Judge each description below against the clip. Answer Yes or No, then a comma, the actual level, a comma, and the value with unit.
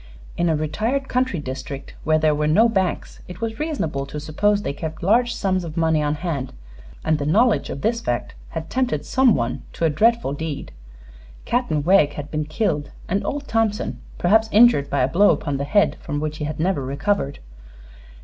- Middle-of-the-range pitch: Yes, medium, 160 Hz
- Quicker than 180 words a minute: Yes, average, 195 wpm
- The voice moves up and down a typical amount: No, wide, 6.7 semitones